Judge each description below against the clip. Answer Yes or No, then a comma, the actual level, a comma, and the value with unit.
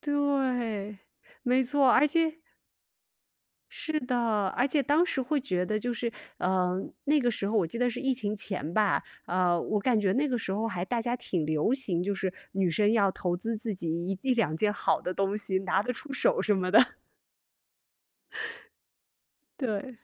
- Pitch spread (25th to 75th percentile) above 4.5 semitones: Yes, average, 5.1 semitones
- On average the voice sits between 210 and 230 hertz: Yes, high, 215 Hz